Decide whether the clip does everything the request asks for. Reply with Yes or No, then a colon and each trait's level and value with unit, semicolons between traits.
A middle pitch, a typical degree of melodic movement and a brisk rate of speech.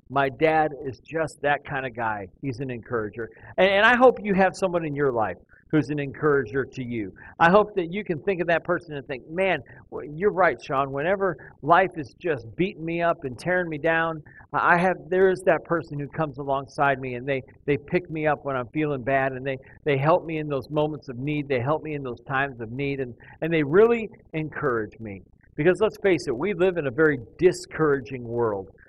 Yes: medium, 150 Hz; average, 4.4 semitones; fast, 225 wpm